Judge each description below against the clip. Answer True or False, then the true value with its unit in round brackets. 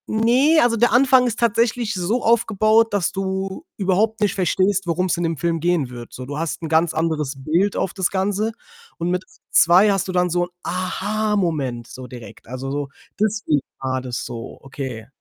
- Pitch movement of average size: False (5.8 semitones)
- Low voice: False (185 Hz)